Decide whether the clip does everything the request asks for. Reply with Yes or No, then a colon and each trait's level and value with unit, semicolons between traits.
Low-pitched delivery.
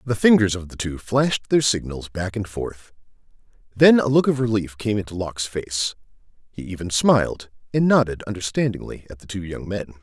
Yes: low, 105 Hz